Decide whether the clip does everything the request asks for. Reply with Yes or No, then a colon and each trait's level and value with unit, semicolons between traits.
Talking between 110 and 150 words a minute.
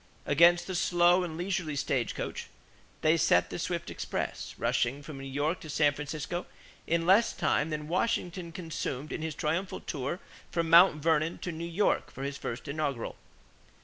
No: average, 165 wpm